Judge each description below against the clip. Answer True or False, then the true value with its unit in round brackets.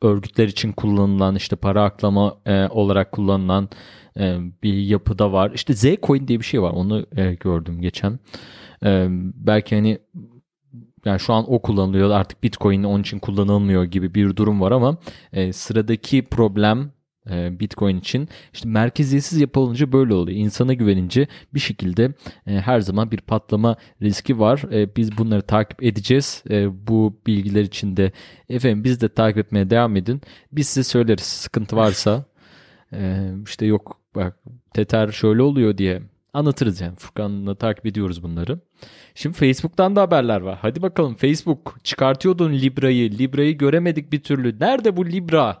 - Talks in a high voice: False (110 Hz)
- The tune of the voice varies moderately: True (4.5 semitones)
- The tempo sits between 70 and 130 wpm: False (140 wpm)